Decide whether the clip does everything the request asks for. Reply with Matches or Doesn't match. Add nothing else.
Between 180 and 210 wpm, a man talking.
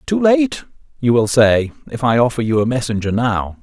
Matches